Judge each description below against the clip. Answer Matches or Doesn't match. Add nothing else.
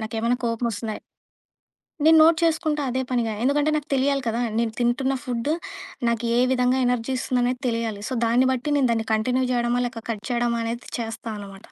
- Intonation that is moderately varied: Doesn't match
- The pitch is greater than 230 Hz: Matches